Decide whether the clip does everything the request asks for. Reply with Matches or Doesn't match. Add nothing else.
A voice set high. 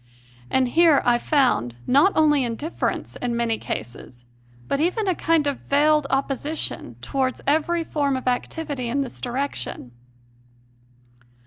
Matches